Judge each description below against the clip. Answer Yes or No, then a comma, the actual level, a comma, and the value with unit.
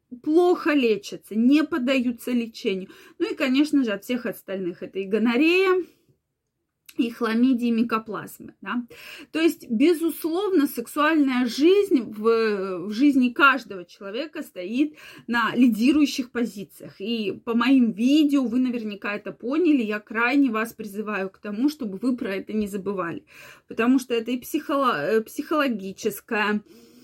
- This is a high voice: Yes, high, 245 Hz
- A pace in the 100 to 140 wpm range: Yes, average, 135 wpm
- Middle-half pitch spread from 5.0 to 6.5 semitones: Yes, average, 5.3 semitones